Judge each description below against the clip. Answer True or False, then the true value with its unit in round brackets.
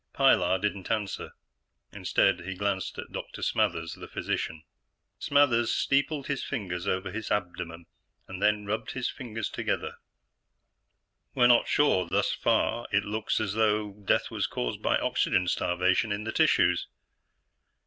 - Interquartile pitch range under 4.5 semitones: True (3.5 semitones)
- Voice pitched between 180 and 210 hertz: False (105 Hz)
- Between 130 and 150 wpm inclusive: True (140 wpm)